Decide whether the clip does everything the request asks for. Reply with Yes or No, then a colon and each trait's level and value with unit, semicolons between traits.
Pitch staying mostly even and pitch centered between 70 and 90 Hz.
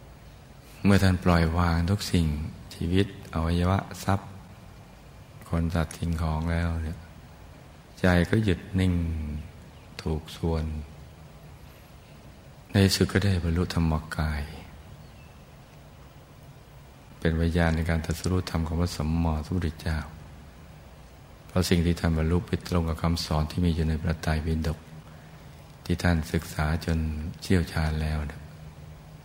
Yes: narrow, 2.3 semitones; very low, 85 Hz